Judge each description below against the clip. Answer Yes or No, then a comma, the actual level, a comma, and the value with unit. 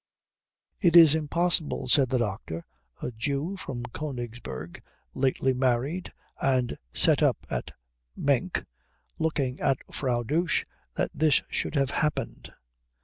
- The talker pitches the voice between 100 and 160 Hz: Yes, low, 135 Hz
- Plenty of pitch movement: No, average, 4.4 semitones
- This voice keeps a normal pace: No, slow, 120 wpm